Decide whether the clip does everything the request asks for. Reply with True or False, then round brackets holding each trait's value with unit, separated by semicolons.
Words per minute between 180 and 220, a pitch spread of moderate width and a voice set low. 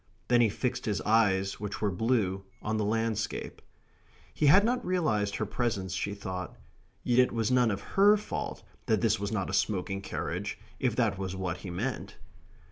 True (185 wpm; 3.9 semitones; 105 Hz)